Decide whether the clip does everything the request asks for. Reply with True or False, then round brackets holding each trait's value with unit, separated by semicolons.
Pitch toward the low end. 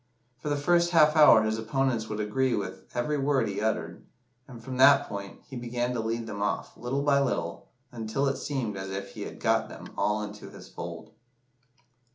True (120 Hz)